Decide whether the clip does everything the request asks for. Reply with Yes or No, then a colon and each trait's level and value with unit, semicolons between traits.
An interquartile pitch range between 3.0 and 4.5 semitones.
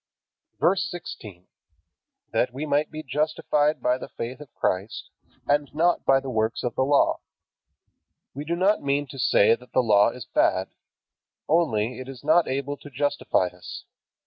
Yes: average, 3.7 semitones